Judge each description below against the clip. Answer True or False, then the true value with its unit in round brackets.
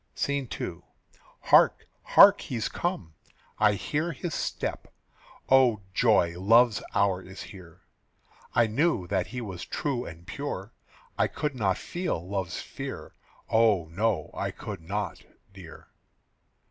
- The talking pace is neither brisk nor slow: False (130 wpm)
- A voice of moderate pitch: False (105 Hz)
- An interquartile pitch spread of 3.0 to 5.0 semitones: False (5.5 semitones)